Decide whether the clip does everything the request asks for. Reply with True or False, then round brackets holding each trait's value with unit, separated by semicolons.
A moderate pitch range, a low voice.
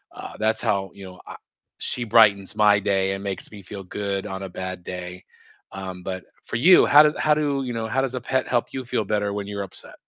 True (3.8 semitones; 100 Hz)